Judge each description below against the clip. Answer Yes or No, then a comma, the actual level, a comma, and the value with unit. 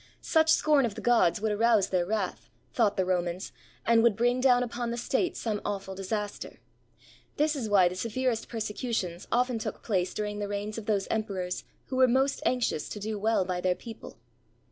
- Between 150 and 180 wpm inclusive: No, average, 190 wpm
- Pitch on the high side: Yes, high, 220 Hz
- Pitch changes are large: No, average, 3.7 semitones